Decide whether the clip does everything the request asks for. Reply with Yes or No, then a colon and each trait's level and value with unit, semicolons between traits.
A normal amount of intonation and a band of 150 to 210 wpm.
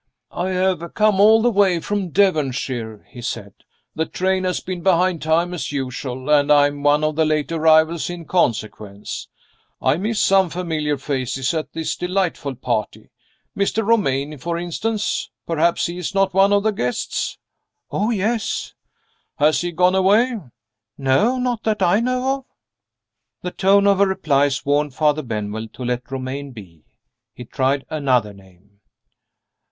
No: wide, 6.2 semitones; average, 155 wpm